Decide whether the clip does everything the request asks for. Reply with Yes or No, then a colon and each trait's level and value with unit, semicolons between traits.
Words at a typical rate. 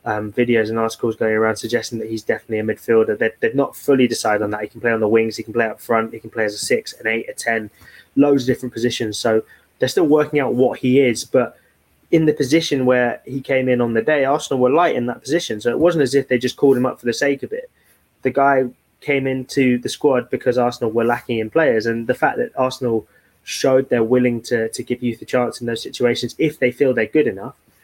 No: fast, 255 wpm